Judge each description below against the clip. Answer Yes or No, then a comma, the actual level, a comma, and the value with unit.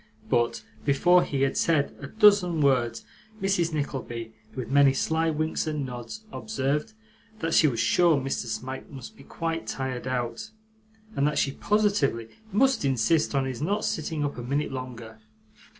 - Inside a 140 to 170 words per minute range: Yes, average, 160 wpm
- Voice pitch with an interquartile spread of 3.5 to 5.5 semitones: Yes, average, 4.4 semitones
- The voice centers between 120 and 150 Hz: Yes, medium, 140 Hz